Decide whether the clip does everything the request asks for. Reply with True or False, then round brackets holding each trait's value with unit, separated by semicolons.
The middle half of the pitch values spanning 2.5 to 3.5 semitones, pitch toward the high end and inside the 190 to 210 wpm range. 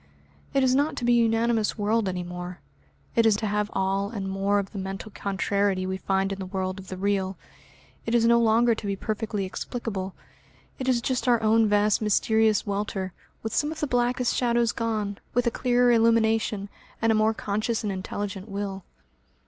True (2.9 semitones; 210 Hz; 195 wpm)